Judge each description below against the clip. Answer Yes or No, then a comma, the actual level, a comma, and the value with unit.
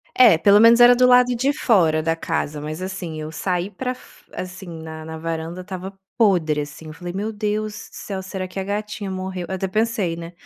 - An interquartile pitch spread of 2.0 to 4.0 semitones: No, average, 4.4 semitones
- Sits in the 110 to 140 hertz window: No, medium, 185 Hz